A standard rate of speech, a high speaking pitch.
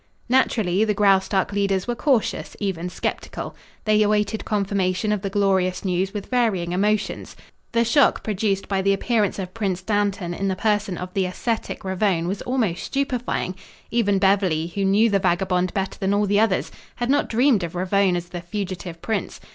Yes: average, 175 wpm; high, 195 Hz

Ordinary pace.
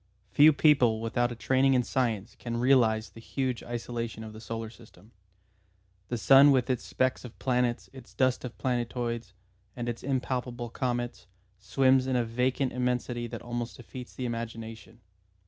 Yes: average, 160 wpm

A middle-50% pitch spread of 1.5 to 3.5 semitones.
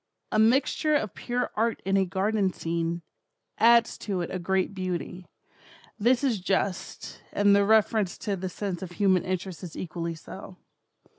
Yes: average, 3.1 semitones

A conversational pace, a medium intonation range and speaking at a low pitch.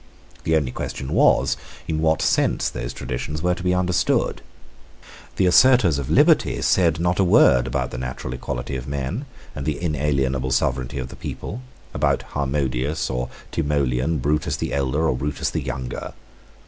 Yes: average, 160 wpm; average, 4.0 semitones; very low, 70 Hz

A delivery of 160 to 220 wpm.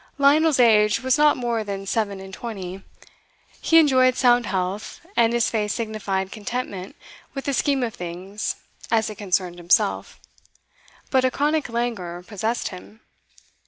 No: average, 145 wpm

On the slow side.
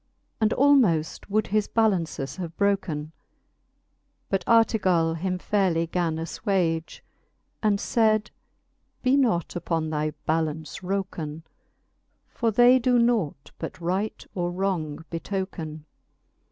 Yes: slow, 110 wpm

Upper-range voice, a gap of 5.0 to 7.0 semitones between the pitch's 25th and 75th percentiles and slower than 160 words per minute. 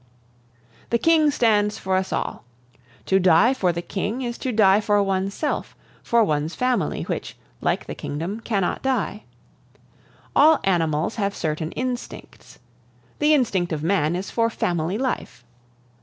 Yes: high, 200 Hz; average, 5.3 semitones; average, 140 wpm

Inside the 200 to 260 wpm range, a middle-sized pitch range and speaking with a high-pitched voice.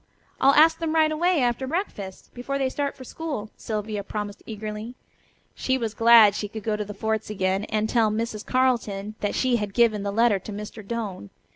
Yes: fast, 205 wpm; average, 3.7 semitones; high, 220 Hz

